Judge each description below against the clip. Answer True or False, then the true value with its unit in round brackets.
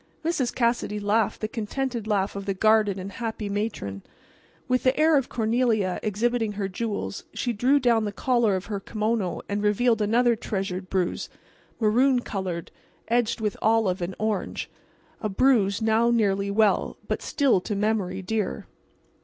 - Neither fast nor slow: True (155 wpm)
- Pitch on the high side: True (215 Hz)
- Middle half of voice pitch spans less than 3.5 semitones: True (3.0 semitones)